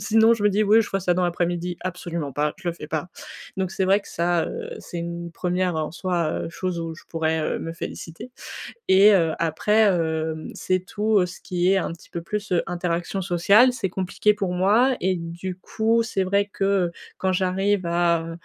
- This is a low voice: No, medium, 180 Hz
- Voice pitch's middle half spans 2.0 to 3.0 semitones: Yes, average, 2.7 semitones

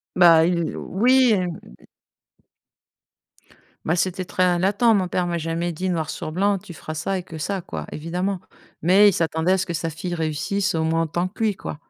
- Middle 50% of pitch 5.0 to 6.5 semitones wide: No, average, 2.7 semitones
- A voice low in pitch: No, medium, 175 Hz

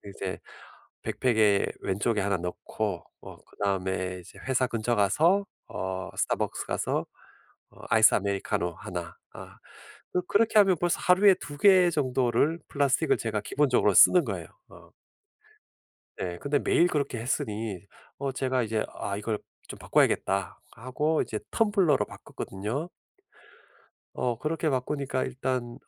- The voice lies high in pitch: No, low, 120 Hz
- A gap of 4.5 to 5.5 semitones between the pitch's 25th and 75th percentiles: No, wide, 6.7 semitones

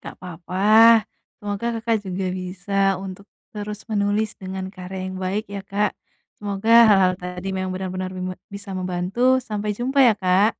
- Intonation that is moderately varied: No, narrow, 2.2 semitones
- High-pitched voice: Yes, high, 195 Hz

